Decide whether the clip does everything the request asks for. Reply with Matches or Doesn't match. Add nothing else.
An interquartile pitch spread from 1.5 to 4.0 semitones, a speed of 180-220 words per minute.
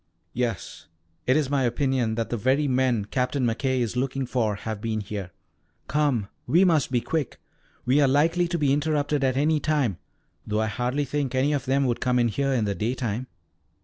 Matches